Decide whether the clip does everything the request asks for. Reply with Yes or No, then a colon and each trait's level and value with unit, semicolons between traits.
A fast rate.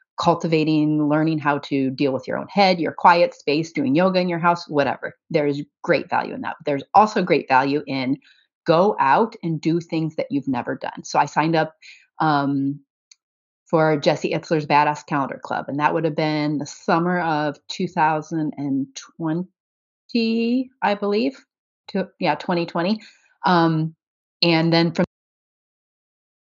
No: average, 150 wpm